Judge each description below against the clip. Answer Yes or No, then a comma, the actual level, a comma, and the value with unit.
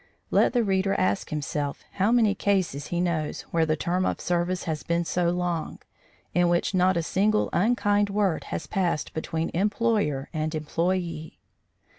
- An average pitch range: Yes, average, 3.5 semitones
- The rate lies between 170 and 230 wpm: No, average, 160 wpm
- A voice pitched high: No, medium, 175 Hz